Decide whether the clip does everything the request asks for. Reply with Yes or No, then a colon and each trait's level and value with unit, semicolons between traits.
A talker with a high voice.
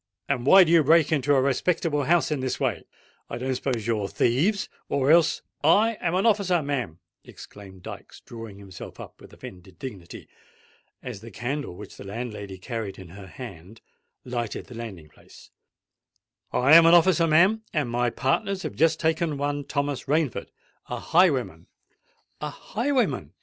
No: low, 135 Hz